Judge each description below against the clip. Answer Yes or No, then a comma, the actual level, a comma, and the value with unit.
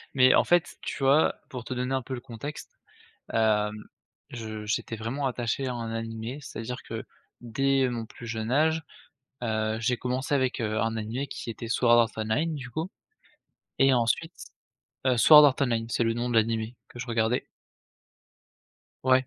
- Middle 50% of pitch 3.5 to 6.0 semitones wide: No, average, 2.8 semitones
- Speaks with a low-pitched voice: Yes, low, 120 Hz